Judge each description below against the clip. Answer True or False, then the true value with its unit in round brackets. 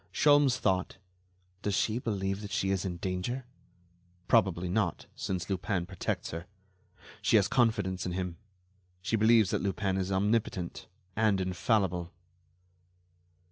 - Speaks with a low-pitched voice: True (95 Hz)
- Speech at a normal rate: False (125 wpm)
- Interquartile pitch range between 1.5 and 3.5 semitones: True (2.9 semitones)